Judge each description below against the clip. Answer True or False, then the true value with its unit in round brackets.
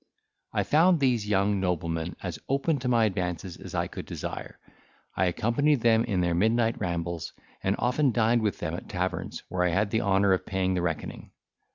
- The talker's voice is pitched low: True (100 Hz)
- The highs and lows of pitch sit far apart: False (4.7 semitones)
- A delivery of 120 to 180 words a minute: False (190 wpm)